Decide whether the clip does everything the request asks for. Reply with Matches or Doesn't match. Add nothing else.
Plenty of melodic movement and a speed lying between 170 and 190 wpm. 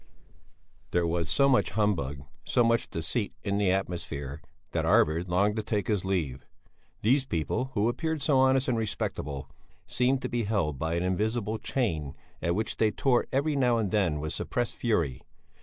Matches